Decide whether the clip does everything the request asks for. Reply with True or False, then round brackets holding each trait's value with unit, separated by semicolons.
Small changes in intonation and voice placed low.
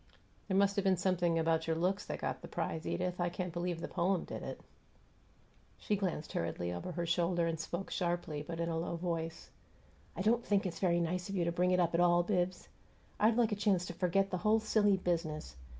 False (2.3 semitones; 175 Hz)